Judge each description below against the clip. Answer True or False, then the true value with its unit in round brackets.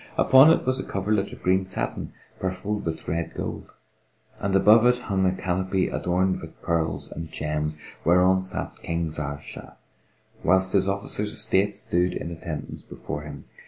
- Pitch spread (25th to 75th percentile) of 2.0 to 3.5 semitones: True (2.9 semitones)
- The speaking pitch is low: True (95 Hz)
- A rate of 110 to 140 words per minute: False (165 wpm)